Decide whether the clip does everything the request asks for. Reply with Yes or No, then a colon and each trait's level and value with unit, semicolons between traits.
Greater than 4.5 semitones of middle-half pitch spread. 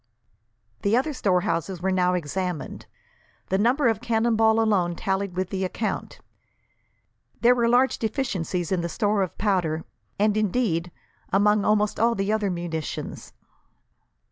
No: average, 3.7 semitones